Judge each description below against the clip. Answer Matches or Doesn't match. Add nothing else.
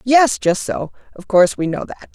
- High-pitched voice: Matches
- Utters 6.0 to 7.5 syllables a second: Doesn't match